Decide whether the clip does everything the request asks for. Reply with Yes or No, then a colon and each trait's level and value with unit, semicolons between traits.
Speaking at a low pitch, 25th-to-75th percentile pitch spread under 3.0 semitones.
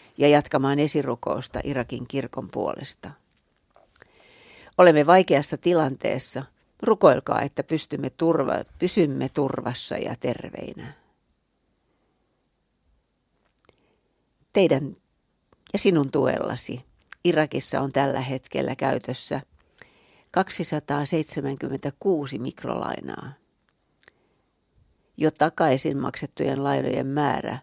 No: medium, 145 Hz; narrow, 2.5 semitones